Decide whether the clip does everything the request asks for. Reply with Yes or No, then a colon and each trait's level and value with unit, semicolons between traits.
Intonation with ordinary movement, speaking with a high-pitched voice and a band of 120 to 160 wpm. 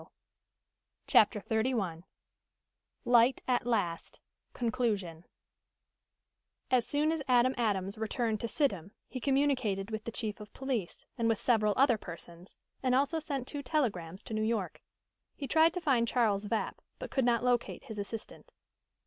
Yes: average, 3.9 semitones; high, 230 Hz; average, 150 wpm